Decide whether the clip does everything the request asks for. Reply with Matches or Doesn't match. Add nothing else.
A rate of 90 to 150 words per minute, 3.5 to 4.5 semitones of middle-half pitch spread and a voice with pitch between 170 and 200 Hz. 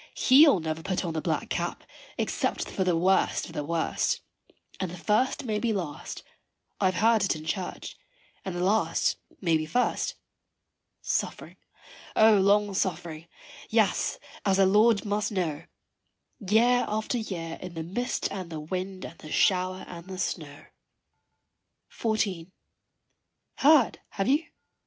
Matches